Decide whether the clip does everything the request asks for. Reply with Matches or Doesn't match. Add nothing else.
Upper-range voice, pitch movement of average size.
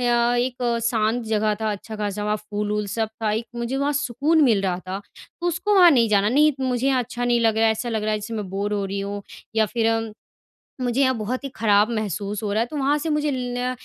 Matches